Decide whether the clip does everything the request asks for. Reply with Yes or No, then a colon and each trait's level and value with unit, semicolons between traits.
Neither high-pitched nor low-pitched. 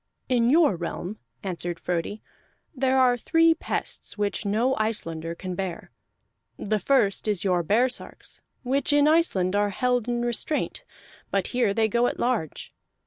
No: high, 220 Hz